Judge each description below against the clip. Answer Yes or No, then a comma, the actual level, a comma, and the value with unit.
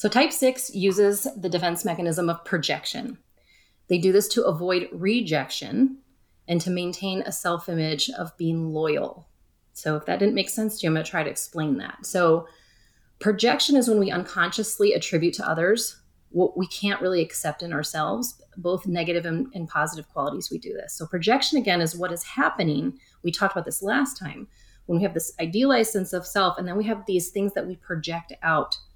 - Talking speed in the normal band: Yes, average, 195 wpm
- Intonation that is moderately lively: Yes, average, 3.9 semitones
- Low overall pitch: No, medium, 180 Hz